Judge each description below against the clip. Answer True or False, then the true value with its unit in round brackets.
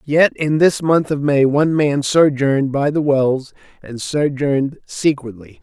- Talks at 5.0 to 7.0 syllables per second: False (4.2 syllables/s)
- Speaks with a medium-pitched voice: True (145 Hz)